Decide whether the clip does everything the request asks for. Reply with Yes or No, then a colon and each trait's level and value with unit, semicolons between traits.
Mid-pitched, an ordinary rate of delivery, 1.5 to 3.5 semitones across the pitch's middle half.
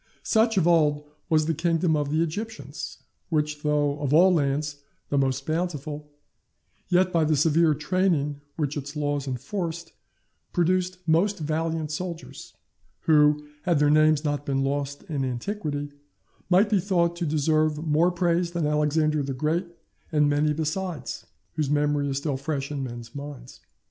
Yes: medium, 155 Hz; average, 155 wpm; narrow, 2.6 semitones